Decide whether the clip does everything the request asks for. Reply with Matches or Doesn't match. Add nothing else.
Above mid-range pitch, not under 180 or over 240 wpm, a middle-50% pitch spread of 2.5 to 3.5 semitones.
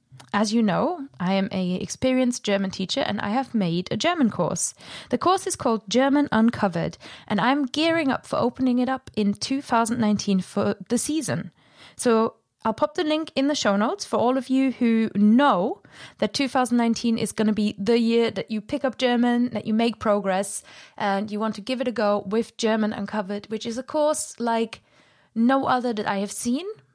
Doesn't match